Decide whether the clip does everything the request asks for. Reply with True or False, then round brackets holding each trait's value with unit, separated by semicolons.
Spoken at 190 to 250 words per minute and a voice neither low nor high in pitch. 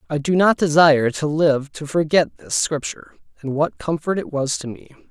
True (200 wpm; 150 Hz)